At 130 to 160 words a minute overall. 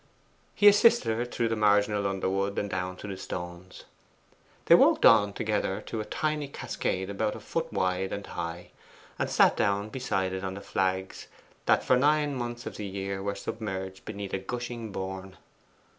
No: average, 175 wpm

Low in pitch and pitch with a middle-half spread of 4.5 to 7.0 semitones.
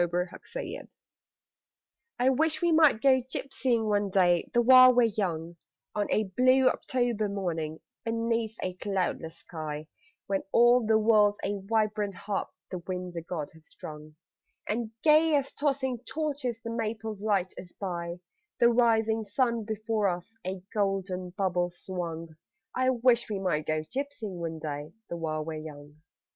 No: high, 205 Hz; average, 5.3 semitones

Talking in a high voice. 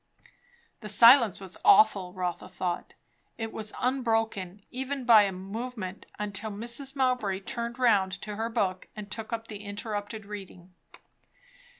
Yes: high, 215 Hz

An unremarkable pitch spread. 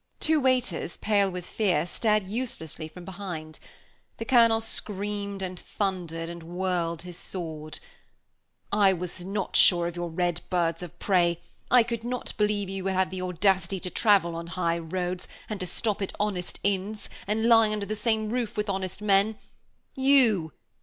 Yes: average, 3.3 semitones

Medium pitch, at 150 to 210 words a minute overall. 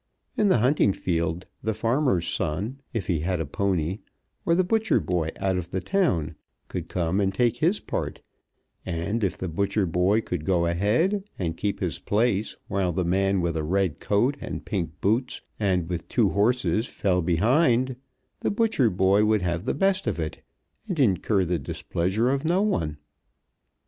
No: low, 100 Hz; average, 175 wpm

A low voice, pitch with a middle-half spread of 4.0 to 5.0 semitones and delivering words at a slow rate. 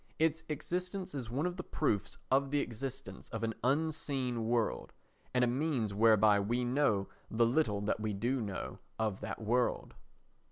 No: low, 125 Hz; average, 4.6 semitones; average, 165 wpm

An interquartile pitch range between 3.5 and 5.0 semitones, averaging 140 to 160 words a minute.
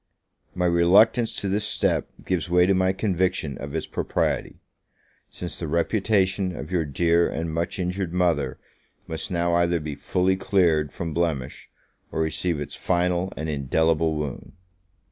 No: average, 2.7 semitones; average, 150 wpm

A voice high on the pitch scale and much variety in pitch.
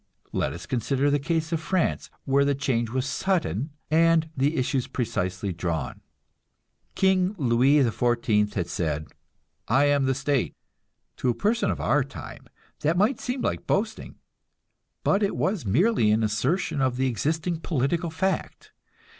No: medium, 140 Hz; wide, 6.1 semitones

